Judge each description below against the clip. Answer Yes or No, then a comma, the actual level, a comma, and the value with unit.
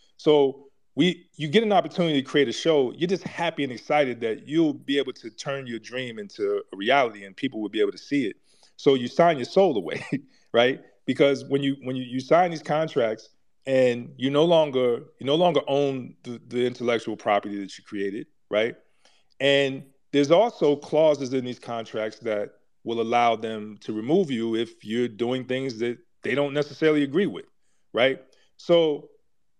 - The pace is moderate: Yes, average, 185 wpm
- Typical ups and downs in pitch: Yes, average, 4.5 semitones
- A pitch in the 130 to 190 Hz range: Yes, low, 135 Hz